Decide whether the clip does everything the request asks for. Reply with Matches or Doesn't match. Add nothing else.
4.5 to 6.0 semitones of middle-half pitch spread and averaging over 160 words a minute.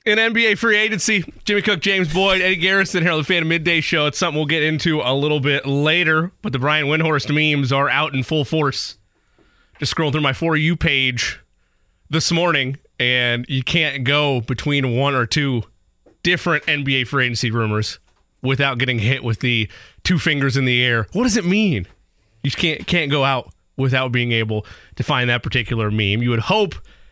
Matches